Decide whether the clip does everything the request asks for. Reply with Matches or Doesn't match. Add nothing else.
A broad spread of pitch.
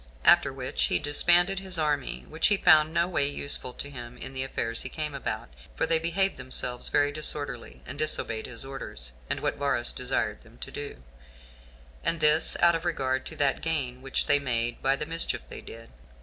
Doesn't match